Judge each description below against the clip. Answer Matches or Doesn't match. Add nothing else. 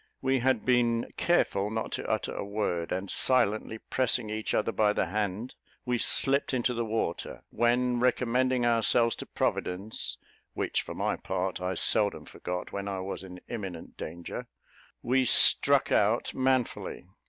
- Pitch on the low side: Matches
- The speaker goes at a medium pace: Matches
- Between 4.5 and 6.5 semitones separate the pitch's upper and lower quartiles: Doesn't match